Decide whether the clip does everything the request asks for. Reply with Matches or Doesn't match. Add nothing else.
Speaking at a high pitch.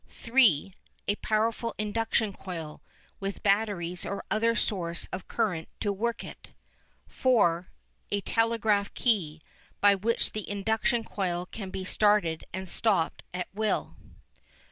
Matches